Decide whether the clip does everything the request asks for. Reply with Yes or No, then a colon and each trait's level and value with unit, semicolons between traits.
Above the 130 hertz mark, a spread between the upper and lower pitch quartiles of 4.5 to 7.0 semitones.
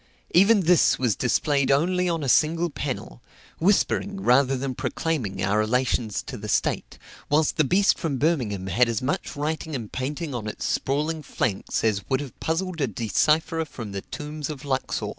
Yes: medium, 140 Hz; average, 5.2 semitones